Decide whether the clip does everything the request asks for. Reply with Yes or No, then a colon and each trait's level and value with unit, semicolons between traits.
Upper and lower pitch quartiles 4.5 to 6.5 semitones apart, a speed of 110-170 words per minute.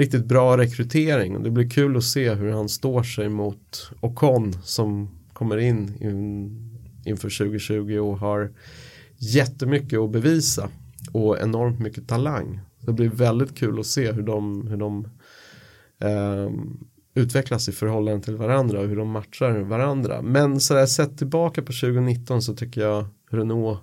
No: average, 3.7 semitones; average, 150 wpm